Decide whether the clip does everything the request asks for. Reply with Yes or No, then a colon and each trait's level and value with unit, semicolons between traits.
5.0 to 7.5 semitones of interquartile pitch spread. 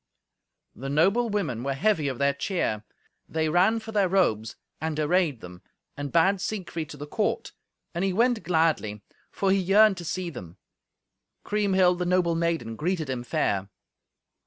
Yes: wide, 5.4 semitones